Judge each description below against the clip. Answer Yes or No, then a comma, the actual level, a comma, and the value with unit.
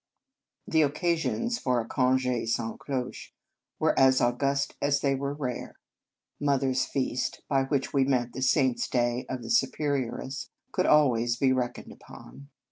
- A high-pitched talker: No, low, 130 Hz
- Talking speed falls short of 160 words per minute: No, average, 165 wpm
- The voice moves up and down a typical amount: No, narrow, 2.1 semitones